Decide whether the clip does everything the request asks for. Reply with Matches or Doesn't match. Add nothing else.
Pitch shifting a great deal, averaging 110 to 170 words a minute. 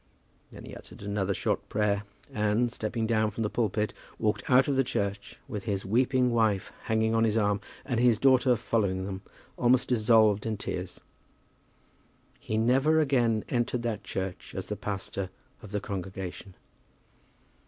Doesn't match